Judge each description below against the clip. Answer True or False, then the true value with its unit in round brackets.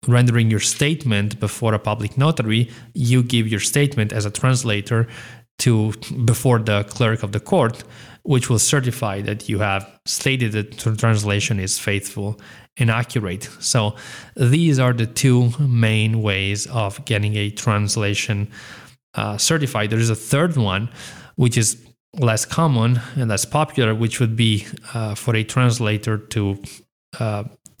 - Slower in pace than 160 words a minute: True (150 wpm)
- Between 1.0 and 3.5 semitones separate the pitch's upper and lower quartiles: True (2.9 semitones)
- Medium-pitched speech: False (115 Hz)